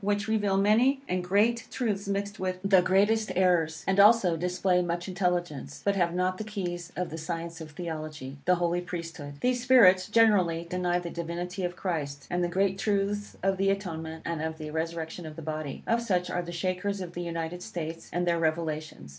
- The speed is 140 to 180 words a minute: No, average, 195 wpm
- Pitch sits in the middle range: Yes, medium, 180 Hz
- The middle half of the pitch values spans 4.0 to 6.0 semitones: No, average, 3.0 semitones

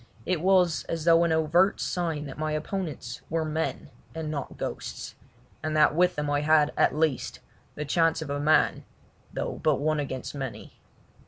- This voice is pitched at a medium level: Yes, medium, 155 Hz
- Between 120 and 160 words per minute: No, average, 175 wpm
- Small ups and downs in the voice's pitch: Yes, narrow, 2.0 semitones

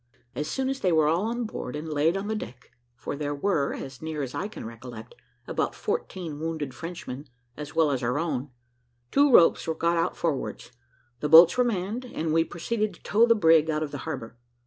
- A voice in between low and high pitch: Yes, medium, 160 Hz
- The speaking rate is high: Yes, fast, 215 wpm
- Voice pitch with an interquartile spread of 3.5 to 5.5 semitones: Yes, average, 5.0 semitones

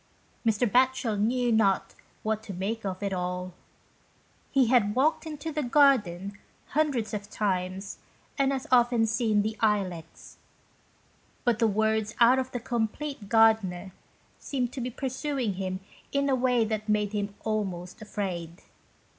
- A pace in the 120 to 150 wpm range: Yes, average, 145 wpm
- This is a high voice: Yes, high, 220 Hz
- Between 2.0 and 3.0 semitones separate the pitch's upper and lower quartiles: No, average, 3.9 semitones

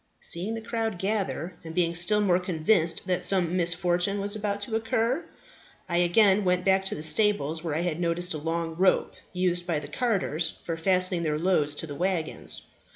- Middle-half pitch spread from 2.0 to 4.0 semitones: Yes, average, 3.2 semitones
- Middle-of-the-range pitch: Yes, medium, 180 Hz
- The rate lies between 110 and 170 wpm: No, average, 190 wpm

